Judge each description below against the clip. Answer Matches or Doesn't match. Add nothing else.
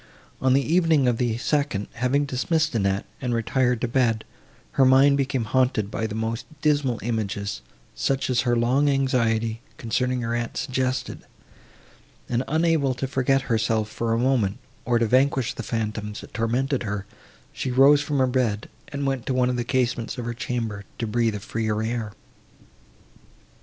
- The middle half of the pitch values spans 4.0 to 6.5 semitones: Doesn't match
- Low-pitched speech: Matches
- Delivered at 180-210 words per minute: Doesn't match